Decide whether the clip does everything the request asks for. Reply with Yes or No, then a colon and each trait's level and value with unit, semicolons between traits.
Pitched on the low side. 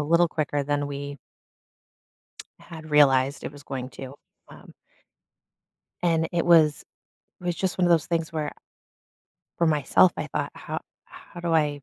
No: medium, 155 Hz